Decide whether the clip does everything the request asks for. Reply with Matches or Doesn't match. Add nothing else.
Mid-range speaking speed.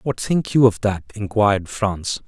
Matches